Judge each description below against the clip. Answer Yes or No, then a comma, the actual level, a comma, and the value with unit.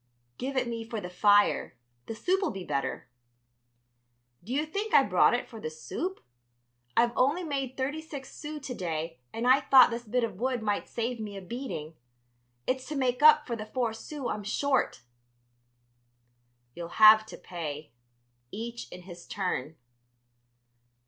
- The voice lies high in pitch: Yes, high, 235 Hz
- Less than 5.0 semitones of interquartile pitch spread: No, wide, 5.4 semitones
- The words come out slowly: No, average, 160 wpm